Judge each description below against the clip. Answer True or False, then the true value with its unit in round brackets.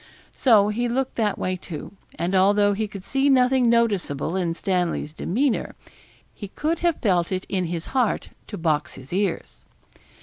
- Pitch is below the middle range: False (200 Hz)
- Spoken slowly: False (165 wpm)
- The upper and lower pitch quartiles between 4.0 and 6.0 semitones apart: True (5.2 semitones)